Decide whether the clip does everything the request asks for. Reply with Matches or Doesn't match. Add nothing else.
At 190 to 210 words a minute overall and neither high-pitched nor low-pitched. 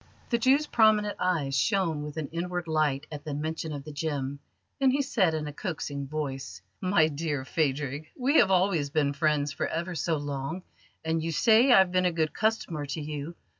Matches